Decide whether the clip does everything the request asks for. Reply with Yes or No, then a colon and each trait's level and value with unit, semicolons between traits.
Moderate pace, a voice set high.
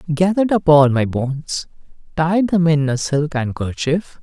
No: average, 155 wpm; medium, 155 Hz